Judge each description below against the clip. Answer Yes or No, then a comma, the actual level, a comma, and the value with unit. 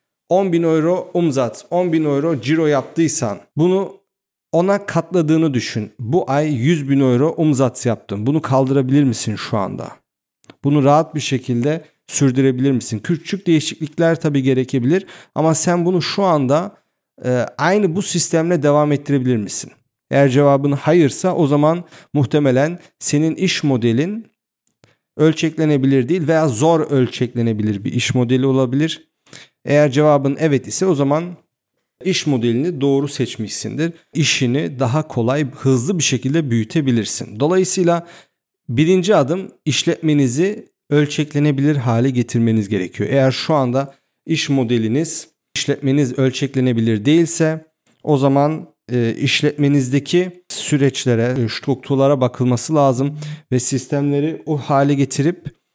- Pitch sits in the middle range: Yes, medium, 145 Hz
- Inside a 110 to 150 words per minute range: Yes, average, 115 wpm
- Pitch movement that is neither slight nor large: Yes, average, 3.6 semitones